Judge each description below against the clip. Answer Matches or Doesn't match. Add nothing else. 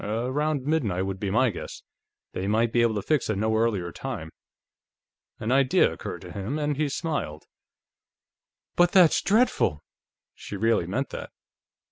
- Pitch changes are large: Matches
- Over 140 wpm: Matches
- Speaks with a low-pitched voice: Matches